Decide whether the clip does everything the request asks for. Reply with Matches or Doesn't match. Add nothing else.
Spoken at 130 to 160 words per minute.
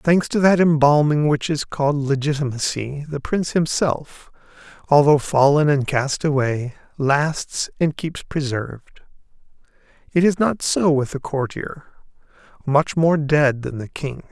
Matches